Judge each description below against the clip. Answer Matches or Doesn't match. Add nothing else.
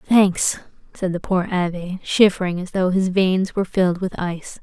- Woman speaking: Matches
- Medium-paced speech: Matches